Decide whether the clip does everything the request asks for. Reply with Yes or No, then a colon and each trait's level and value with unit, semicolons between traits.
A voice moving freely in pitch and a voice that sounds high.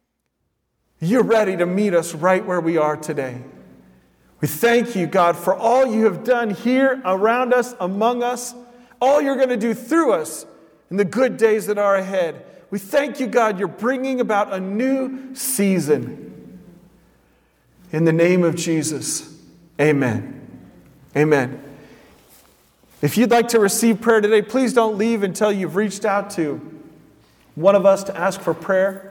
Yes: wide, 6.0 semitones; high, 200 Hz